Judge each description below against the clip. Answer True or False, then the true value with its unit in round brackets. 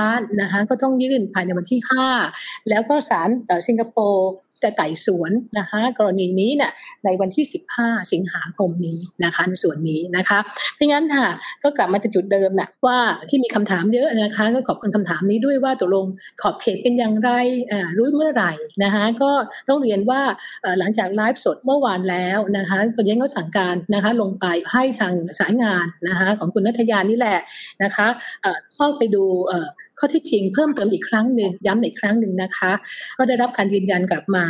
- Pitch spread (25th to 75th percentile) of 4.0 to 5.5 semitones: True (4.6 semitones)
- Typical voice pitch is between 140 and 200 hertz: False (215 Hz)